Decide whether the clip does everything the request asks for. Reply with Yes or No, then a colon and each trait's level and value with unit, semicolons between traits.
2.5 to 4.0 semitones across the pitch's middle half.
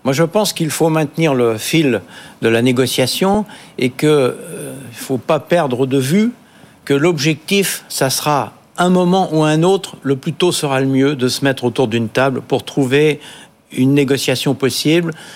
No: average, 4.4 semitones